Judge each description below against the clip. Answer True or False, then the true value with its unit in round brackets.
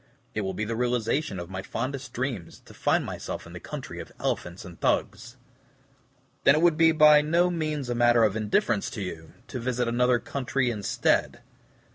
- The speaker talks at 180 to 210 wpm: True (185 wpm)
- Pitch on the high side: False (120 Hz)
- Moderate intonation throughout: True (4.8 semitones)